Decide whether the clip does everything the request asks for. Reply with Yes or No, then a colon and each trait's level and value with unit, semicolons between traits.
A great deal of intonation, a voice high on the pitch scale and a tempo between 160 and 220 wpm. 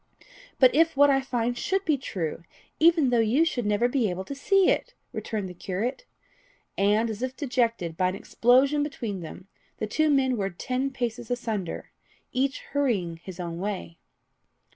Yes: wide, 5.7 semitones; high, 240 Hz; average, 170 wpm